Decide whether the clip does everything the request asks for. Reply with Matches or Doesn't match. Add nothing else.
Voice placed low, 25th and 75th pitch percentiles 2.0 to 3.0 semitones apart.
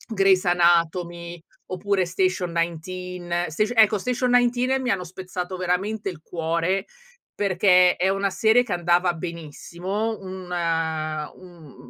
Doesn't match